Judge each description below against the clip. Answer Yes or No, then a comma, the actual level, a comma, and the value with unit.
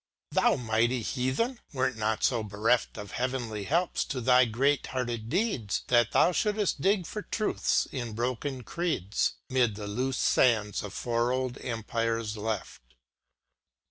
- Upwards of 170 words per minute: No, average, 145 wpm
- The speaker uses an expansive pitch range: No, average, 3.1 semitones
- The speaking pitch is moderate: No, low, 120 Hz